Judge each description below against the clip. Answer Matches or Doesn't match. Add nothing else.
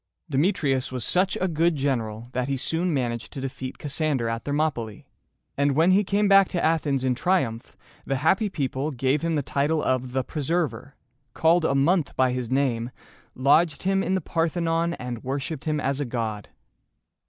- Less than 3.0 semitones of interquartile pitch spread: Doesn't match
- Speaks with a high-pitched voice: Doesn't match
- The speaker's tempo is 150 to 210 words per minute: Matches